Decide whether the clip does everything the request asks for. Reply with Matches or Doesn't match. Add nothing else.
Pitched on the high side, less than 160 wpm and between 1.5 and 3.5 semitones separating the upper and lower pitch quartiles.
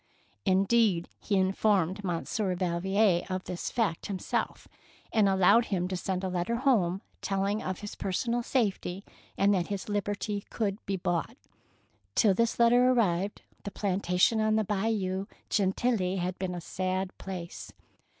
Matches